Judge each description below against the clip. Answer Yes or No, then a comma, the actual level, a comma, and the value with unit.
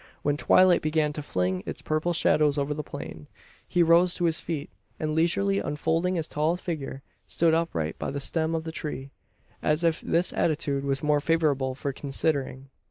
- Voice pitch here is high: No, medium, 155 Hz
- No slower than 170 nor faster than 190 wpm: Yes, average, 180 wpm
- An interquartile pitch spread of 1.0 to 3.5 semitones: Yes, average, 2.9 semitones